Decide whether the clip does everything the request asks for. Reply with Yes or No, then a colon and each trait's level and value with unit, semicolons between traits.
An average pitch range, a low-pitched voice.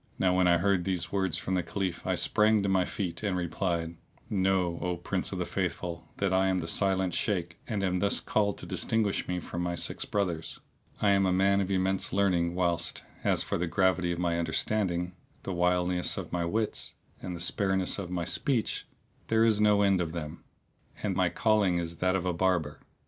No: narrow, 2.1 semitones; very low, 90 Hz